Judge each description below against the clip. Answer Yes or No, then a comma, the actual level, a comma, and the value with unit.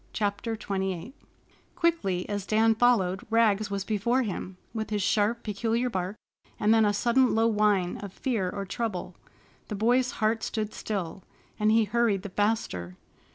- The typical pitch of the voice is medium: No, high, 215 Hz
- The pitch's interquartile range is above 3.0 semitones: No, narrow, 2.6 semitones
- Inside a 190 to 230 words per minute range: No, average, 155 wpm